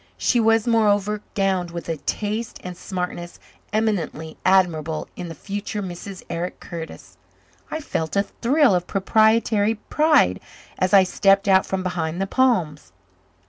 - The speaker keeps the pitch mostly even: No, average, 3.8 semitones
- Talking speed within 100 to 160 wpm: Yes, average, 140 wpm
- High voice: Yes, high, 195 Hz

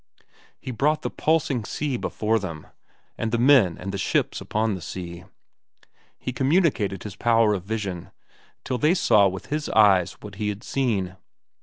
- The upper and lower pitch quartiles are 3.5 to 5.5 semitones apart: Yes, average, 5.1 semitones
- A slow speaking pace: No, average, 165 wpm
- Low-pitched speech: Yes, low, 110 Hz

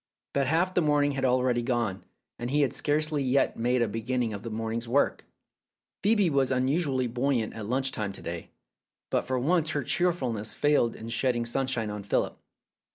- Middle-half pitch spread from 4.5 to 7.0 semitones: No, average, 3.7 semitones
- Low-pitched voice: Yes, low, 130 Hz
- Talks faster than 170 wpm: Yes, average, 180 wpm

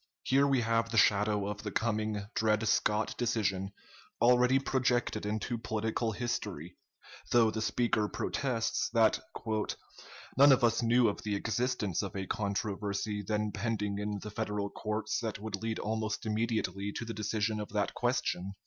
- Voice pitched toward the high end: No, low, 110 Hz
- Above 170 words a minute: No, average, 155 wpm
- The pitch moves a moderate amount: No, narrow, 2.1 semitones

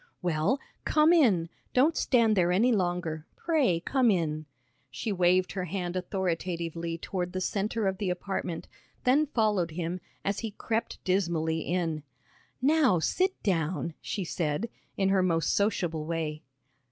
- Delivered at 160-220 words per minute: No, average, 140 wpm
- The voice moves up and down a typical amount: Yes, average, 4.4 semitones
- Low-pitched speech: No, medium, 185 Hz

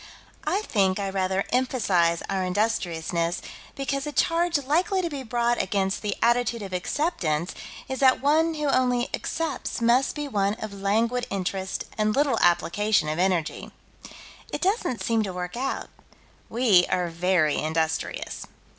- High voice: Yes, high, 215 Hz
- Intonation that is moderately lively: No, wide, 6.3 semitones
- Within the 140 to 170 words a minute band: Yes, average, 145 wpm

